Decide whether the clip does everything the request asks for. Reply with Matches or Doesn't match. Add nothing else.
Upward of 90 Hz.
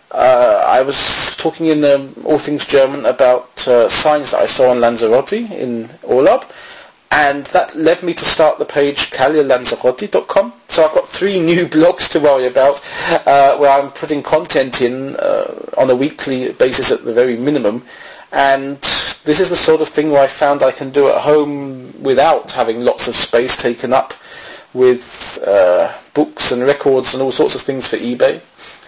Matches